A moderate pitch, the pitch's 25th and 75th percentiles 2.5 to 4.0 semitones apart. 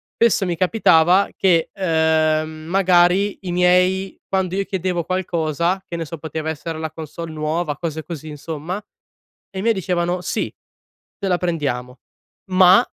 Yes: medium, 175 Hz; average, 2.8 semitones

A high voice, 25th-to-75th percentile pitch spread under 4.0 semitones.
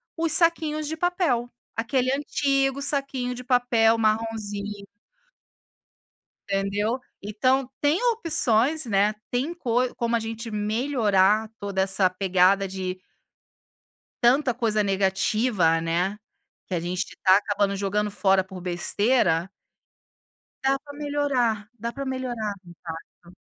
No: high, 225 Hz; average, 5.1 semitones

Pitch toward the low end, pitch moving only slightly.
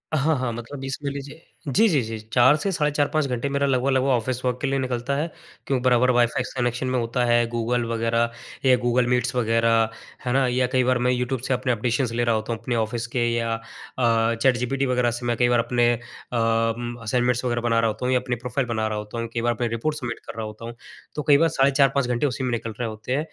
Yes: low, 120 Hz; narrow, 1.9 semitones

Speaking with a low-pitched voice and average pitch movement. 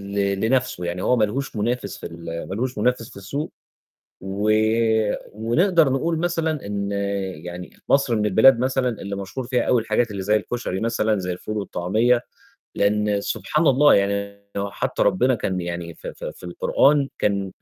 Yes: low, 105 Hz; average, 4.4 semitones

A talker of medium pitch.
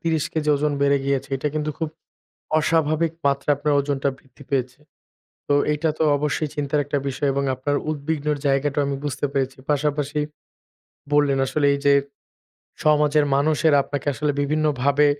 Yes: medium, 145 Hz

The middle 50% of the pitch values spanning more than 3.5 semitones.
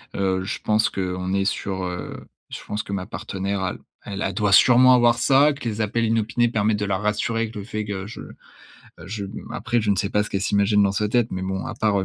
No: narrow, 2.4 semitones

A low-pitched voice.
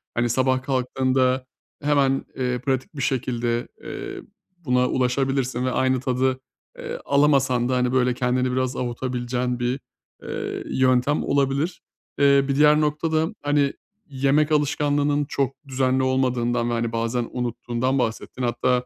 Yes: low, 130 Hz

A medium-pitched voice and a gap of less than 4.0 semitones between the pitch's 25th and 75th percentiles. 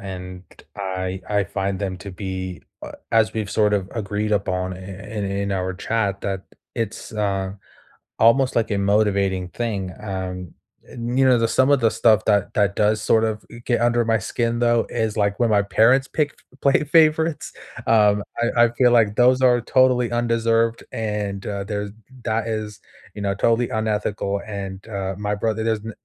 No: low, 105 Hz; average, 2.8 semitones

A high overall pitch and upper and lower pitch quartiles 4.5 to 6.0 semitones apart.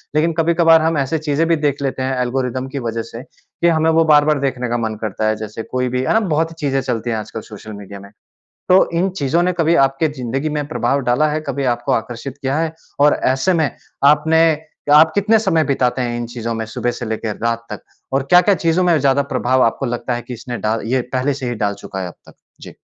No: low, 135 Hz; average, 5.0 semitones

